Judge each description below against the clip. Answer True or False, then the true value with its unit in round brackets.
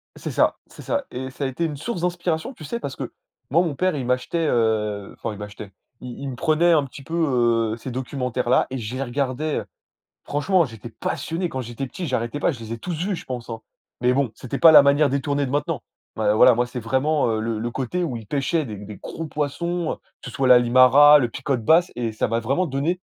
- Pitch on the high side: False (135 Hz)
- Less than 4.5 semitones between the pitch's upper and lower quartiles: False (4.8 semitones)